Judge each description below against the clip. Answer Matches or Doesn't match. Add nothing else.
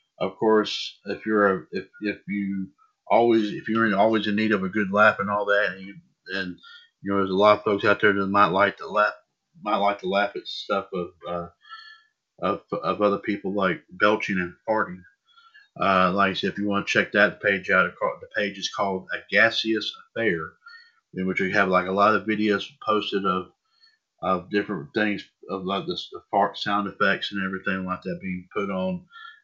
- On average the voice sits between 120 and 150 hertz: Doesn't match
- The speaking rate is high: Matches